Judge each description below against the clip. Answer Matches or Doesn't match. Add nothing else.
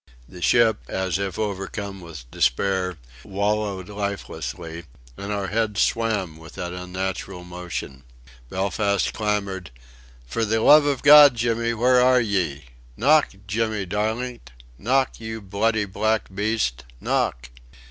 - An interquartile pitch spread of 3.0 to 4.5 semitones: Matches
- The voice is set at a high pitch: Doesn't match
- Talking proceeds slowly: Matches